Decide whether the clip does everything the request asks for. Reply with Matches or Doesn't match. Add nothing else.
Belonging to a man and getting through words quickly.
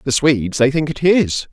Matches